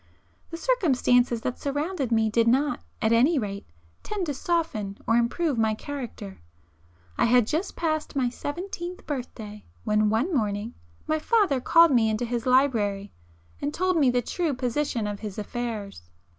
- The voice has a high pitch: Yes, very high, 250 Hz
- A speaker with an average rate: Yes, average, 155 wpm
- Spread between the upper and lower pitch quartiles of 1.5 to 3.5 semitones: No, wide, 5.6 semitones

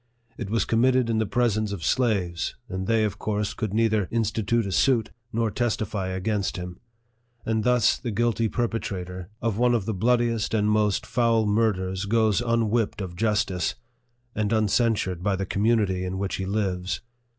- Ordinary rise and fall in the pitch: Yes, average, 3.1 semitones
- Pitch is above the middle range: No, low, 110 Hz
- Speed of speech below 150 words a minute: No, average, 180 wpm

